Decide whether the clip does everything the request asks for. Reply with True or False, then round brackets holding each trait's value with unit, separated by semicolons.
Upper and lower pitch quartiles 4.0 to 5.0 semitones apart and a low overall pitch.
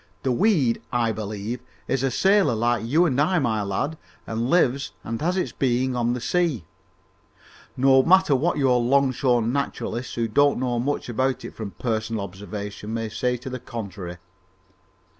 False (3.6 semitones; 125 Hz)